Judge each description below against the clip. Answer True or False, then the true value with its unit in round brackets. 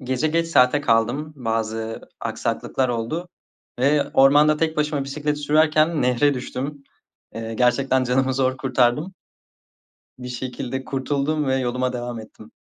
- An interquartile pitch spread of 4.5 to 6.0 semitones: False (3.2 semitones)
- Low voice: True (130 Hz)